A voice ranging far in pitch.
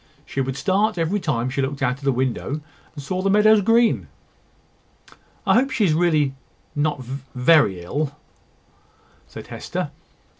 Yes: wide, 6.7 semitones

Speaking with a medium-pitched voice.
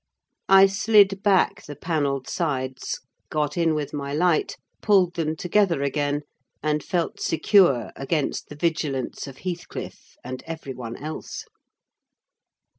Yes: medium, 155 Hz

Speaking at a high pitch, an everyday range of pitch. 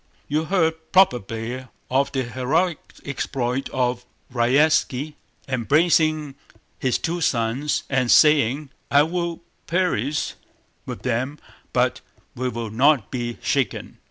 No: low, 135 Hz; average, 4.0 semitones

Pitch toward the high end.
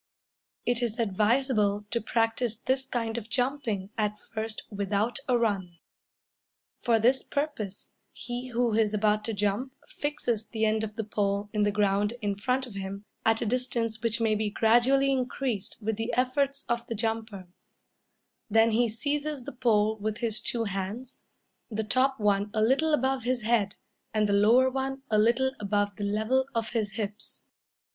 Yes: high, 225 Hz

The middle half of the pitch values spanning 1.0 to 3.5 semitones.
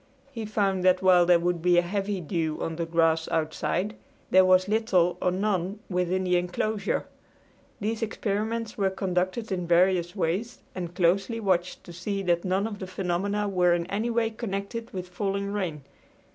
Yes: average, 2.7 semitones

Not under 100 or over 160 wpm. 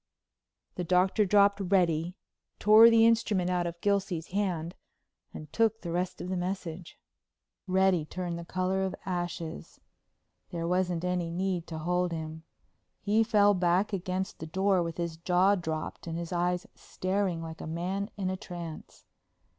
Yes: average, 155 wpm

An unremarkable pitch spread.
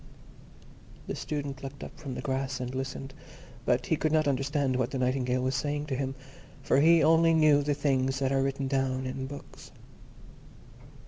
No: narrow, 1.8 semitones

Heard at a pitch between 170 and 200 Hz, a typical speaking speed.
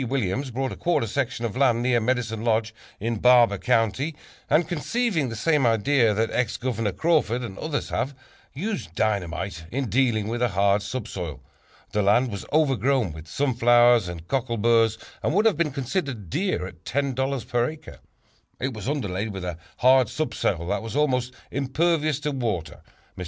No: low, 120 Hz; average, 170 wpm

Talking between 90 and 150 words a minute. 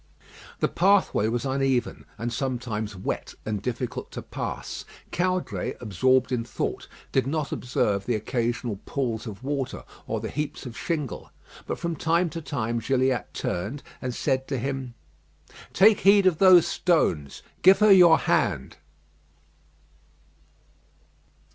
Yes: slow, 135 wpm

